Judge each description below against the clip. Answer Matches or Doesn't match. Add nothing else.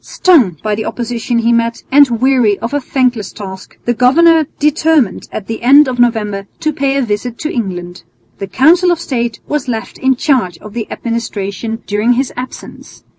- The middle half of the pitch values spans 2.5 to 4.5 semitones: Matches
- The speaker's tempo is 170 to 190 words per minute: Matches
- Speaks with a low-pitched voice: Doesn't match